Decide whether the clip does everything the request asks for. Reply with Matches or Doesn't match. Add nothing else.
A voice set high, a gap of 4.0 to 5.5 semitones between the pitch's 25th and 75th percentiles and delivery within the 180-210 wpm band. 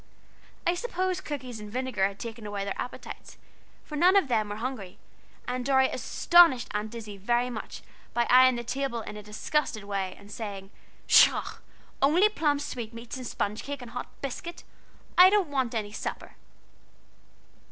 Doesn't match